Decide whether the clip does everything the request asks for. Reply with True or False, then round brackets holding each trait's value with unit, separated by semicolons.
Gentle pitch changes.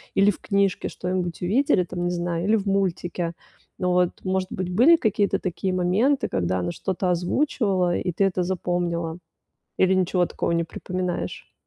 True (1.8 semitones)